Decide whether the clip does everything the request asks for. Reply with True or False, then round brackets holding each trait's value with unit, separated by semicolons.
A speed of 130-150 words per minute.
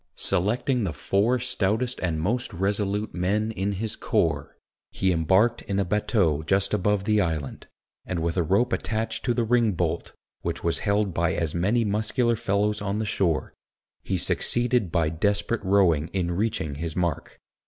False (165 wpm)